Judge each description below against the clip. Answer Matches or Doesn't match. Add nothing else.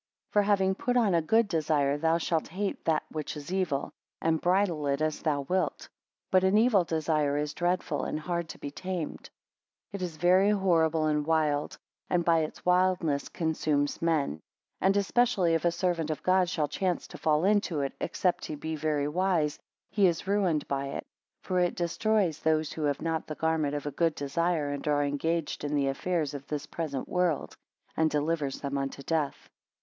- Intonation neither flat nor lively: Matches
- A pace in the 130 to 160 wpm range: Doesn't match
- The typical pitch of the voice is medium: Matches